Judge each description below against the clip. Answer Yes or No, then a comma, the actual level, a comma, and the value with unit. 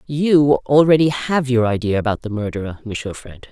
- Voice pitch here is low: Yes, low, 125 Hz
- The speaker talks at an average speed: Yes, average, 170 wpm